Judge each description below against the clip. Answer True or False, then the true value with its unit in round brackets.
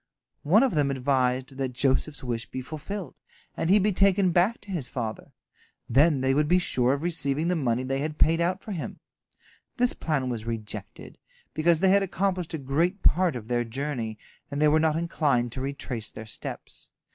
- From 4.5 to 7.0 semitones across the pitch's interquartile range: True (5.3 semitones)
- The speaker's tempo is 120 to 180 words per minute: False (190 wpm)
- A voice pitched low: False (150 Hz)